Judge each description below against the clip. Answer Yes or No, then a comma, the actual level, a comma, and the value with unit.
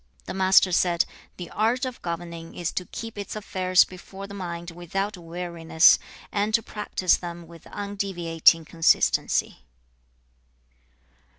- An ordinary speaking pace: No, slow, 125 wpm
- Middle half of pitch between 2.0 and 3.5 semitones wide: Yes, average, 2.9 semitones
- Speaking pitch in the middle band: Yes, medium, 180 Hz